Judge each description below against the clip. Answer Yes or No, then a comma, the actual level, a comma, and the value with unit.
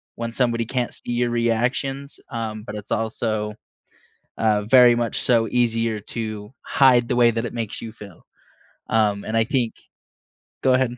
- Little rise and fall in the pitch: Yes, narrow, 1.9 semitones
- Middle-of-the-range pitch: No, low, 115 Hz